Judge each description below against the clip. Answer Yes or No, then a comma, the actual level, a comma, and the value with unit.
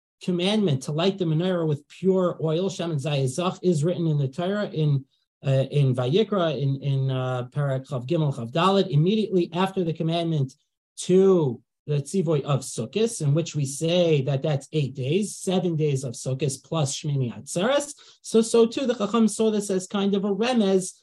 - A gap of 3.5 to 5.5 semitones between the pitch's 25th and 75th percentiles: Yes, average, 5.2 semitones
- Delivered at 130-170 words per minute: No, average, 185 wpm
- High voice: No, medium, 165 Hz